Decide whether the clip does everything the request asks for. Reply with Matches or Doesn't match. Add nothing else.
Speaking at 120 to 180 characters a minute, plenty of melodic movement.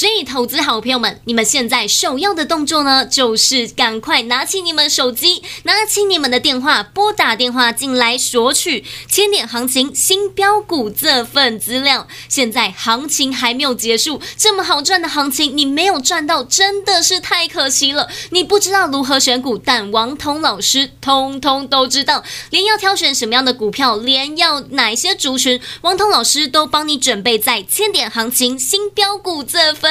Doesn't match